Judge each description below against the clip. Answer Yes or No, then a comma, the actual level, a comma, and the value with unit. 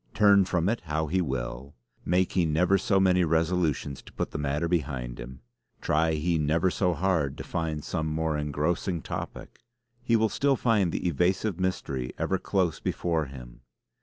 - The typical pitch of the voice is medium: No, very low, 80 Hz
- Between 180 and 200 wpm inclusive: No, average, 170 wpm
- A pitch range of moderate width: Yes, average, 3.9 semitones